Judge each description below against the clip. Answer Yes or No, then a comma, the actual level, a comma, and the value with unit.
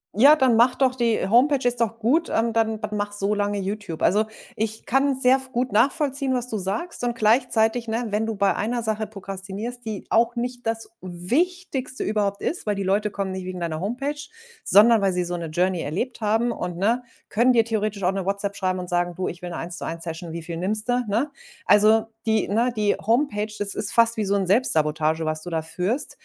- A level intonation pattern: No, average, 3.9 semitones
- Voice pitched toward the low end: No, high, 215 Hz